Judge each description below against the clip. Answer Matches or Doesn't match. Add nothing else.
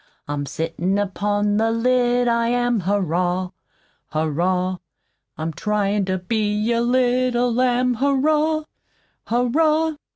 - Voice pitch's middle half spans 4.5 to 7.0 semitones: Matches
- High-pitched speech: Matches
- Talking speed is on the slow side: Matches